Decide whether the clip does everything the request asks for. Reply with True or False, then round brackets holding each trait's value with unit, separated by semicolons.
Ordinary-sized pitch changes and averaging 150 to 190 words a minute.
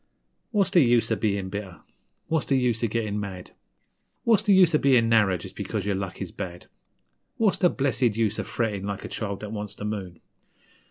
False (5.0 semitones; 205 wpm)